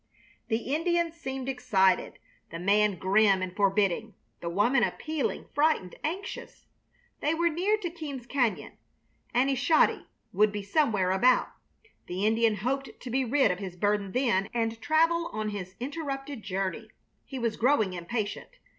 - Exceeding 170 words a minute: No, average, 145 wpm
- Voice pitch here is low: No, high, 230 Hz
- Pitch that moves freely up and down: Yes, wide, 6.2 semitones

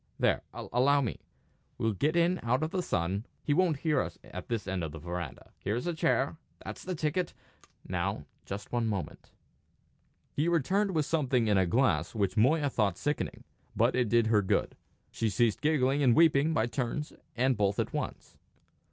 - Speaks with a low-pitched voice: Yes, low, 130 Hz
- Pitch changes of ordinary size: No, wide, 6.4 semitones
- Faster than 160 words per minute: Yes, average, 180 wpm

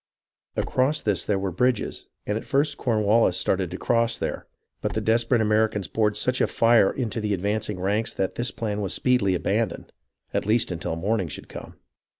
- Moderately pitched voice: No, low, 105 Hz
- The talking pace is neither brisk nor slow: Yes, average, 180 wpm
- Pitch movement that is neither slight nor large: Yes, average, 3.1 semitones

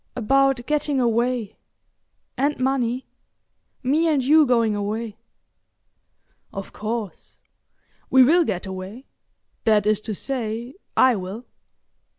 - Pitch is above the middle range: Yes, high, 240 Hz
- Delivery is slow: Yes, slow, 100 wpm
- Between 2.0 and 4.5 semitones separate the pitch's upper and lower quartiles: Yes, average, 3.9 semitones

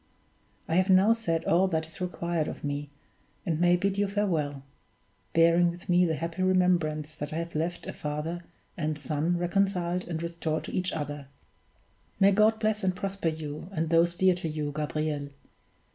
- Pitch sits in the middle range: Yes, medium, 170 Hz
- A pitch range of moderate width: Yes, average, 3.0 semitones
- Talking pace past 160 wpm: Yes, average, 175 wpm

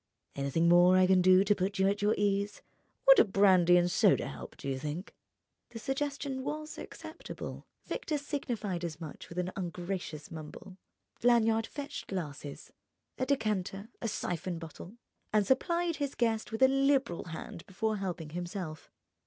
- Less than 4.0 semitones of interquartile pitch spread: No, wide, 5.4 semitones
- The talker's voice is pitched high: Yes, high, 195 Hz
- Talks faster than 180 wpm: No, average, 160 wpm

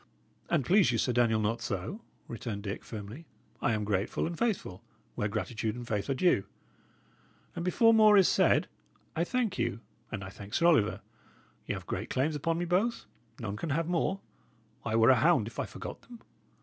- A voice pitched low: Yes, low, 125 Hz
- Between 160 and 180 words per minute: No, average, 190 wpm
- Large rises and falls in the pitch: Yes, wide, 8.4 semitones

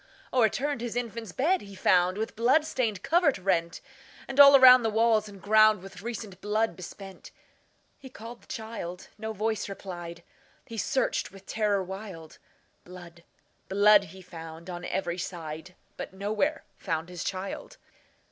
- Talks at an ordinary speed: No, slow, 125 wpm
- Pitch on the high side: Yes, high, 205 Hz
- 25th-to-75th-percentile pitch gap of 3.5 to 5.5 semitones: Yes, average, 4.0 semitones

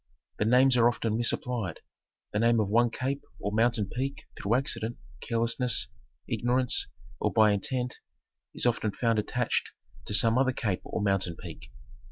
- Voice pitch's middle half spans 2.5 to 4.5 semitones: Yes, average, 2.8 semitones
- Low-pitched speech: Yes, low, 115 Hz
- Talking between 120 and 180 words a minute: Yes, average, 155 wpm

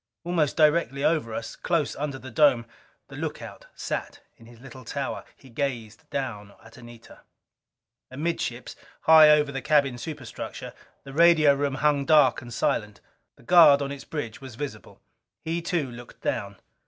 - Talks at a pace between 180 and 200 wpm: No, average, 155 wpm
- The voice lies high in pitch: No, medium, 140 Hz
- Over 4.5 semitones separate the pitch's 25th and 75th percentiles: No, average, 4.1 semitones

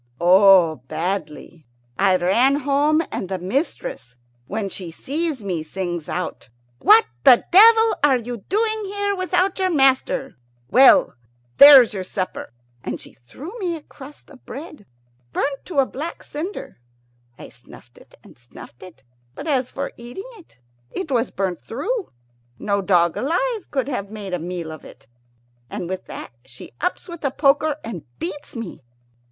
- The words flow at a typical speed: Yes, average, 160 wpm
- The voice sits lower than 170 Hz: No, very high, 255 Hz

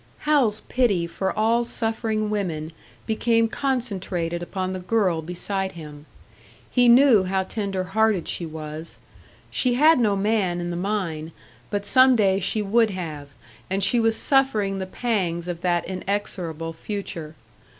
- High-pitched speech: Yes, high, 195 Hz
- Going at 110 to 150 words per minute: Yes, average, 140 wpm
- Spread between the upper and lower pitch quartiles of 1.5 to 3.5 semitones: No, average, 4.4 semitones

